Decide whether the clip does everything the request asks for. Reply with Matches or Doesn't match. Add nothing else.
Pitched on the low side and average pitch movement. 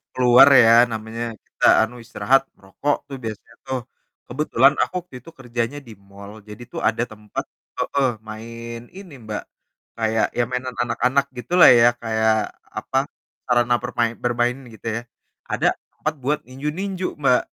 Matches